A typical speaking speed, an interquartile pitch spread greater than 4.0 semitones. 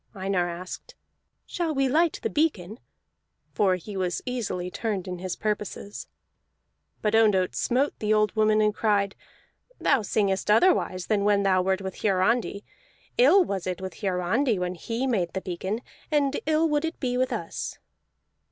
Yes: average, 160 wpm; average, 4.9 semitones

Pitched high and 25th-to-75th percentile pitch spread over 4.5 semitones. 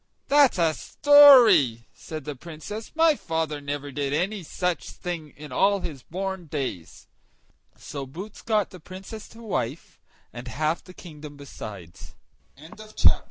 No: medium, 160 Hz; wide, 5.5 semitones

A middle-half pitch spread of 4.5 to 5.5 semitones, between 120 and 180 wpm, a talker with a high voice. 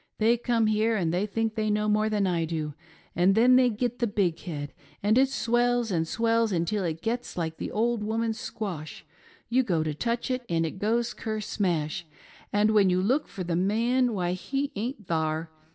No: average, 4.9 semitones; average, 200 wpm; high, 210 Hz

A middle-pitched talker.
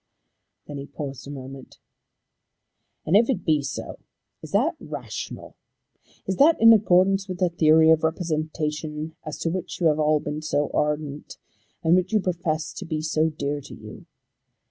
Yes: medium, 155 Hz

